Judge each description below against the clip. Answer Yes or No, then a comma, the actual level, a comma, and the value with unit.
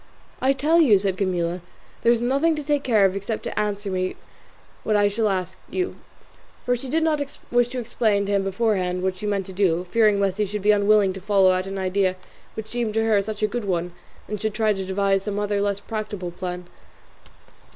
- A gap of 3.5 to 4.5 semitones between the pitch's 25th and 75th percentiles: No, average, 2.7 semitones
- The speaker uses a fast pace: Yes, fast, 220 wpm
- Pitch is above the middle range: Yes, high, 205 Hz